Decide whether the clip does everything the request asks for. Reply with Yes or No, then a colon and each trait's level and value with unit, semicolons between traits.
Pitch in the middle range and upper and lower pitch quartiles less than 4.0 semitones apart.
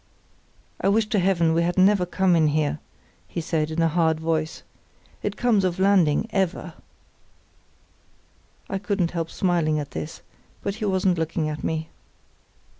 Yes: medium, 170 Hz; average, 3.2 semitones